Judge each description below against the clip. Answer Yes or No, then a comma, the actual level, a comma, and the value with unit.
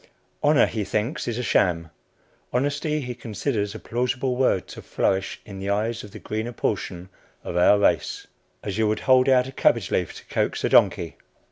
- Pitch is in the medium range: No, low, 110 Hz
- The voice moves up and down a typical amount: Yes, average, 4.0 semitones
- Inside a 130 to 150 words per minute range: No, average, 190 wpm